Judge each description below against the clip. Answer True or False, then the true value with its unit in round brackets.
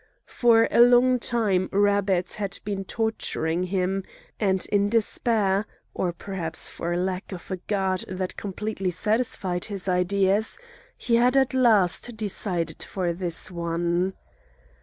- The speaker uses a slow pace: True (130 wpm)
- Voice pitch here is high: True (195 Hz)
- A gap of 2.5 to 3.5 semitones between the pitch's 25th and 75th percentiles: True (3.2 semitones)